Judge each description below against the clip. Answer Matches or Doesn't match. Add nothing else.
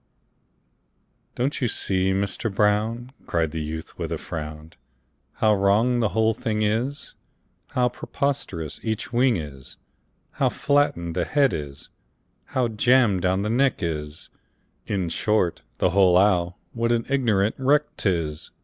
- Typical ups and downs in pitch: Doesn't match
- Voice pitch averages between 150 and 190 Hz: Doesn't match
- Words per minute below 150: Matches